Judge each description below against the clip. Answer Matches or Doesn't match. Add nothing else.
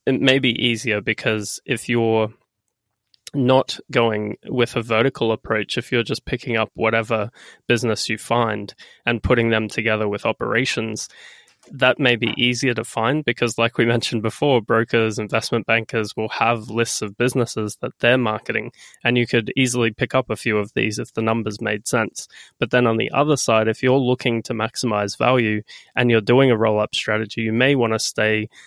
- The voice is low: Matches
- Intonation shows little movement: Matches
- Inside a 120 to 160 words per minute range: Doesn't match